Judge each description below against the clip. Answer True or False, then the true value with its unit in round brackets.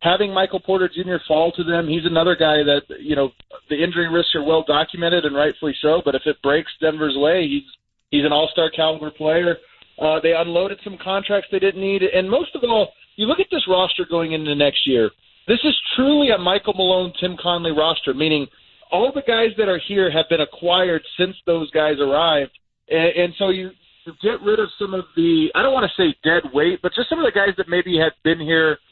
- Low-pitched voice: False (175 Hz)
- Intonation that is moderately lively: True (3.6 semitones)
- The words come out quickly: True (220 wpm)